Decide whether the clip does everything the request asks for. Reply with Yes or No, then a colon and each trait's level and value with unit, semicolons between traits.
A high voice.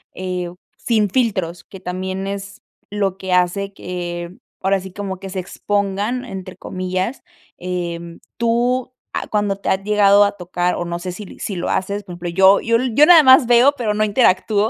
Yes: high, 195 Hz